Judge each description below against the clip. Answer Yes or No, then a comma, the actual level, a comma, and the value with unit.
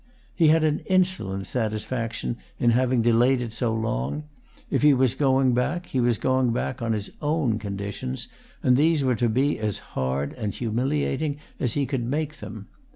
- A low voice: Yes, low, 125 Hz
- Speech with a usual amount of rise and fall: Yes, average, 4.4 semitones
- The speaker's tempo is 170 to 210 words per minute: Yes, average, 175 wpm